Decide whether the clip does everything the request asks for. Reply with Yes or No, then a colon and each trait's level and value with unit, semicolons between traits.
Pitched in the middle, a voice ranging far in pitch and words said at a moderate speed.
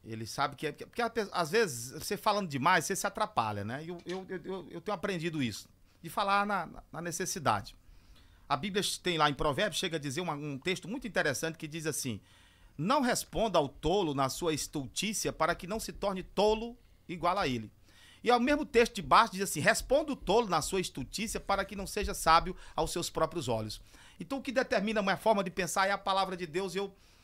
No: medium, 180 Hz; wide, 5.8 semitones; fast, 220 wpm